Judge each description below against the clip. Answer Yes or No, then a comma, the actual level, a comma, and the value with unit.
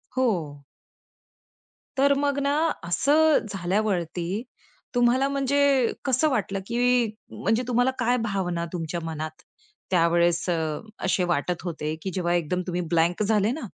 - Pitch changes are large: Yes, wide, 6.4 semitones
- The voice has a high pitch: Yes, high, 195 Hz